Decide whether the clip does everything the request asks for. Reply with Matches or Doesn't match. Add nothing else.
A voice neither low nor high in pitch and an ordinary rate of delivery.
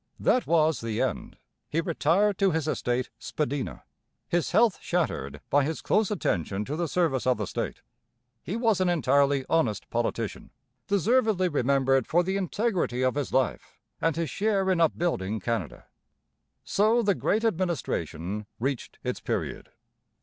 Matches